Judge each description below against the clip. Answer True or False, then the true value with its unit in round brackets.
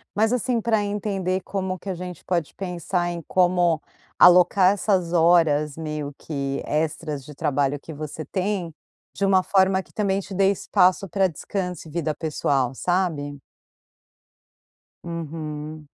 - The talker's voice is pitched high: False (175 Hz)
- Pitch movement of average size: True (3.8 semitones)